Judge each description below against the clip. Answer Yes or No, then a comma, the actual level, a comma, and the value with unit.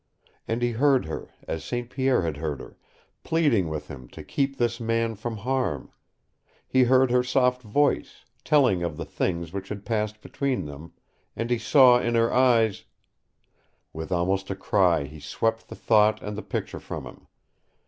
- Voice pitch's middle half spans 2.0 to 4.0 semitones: No, wide, 5.5 semitones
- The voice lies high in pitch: No, low, 115 Hz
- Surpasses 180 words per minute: No, average, 175 wpm